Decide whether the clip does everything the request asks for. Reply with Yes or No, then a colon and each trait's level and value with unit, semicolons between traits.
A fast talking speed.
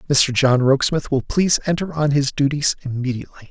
No: average, 170 wpm